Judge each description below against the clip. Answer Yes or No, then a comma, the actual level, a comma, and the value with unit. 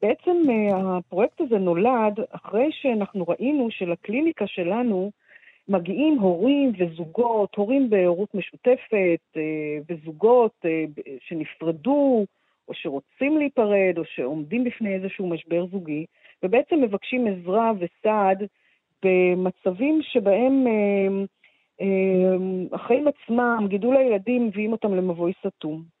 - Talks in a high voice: Yes, high, 200 Hz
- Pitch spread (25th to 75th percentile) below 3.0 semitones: No, average, 5.1 semitones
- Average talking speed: No, slow, 90 wpm